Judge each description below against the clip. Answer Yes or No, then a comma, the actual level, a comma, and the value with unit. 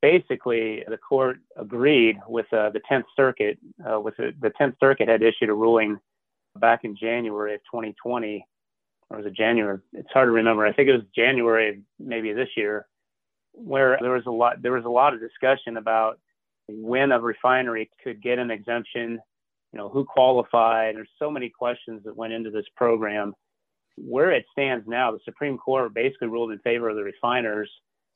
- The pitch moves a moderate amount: No, narrow, 2.3 semitones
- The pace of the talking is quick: No, average, 185 wpm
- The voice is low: Yes, low, 115 Hz